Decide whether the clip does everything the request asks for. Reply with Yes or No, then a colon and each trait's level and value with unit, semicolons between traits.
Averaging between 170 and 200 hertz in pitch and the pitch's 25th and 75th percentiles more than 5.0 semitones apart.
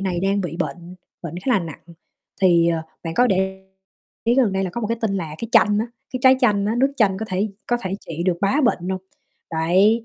No: high, 195 Hz; average, 4.3 semitones